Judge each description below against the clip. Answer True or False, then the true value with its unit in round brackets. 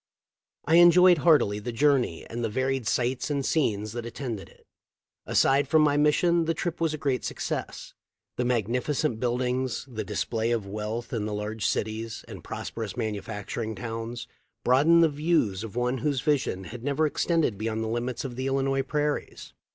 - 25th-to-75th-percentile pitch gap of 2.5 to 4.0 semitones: False (4.6 semitones)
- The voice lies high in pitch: False (125 Hz)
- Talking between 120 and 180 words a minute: True (170 wpm)